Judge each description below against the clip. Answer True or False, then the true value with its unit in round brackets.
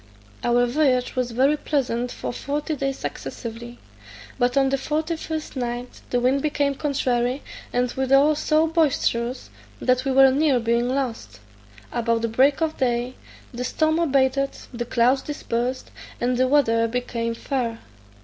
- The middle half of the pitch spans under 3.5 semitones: True (2.7 semitones)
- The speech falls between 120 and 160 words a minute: True (145 wpm)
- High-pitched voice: True (255 Hz)